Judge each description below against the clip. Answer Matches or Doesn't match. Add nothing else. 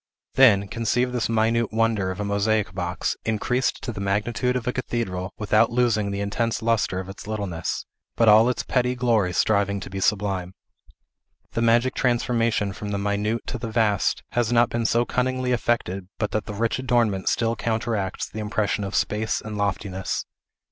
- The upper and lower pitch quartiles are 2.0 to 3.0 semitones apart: Matches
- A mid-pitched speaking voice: Doesn't match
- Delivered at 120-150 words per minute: Doesn't match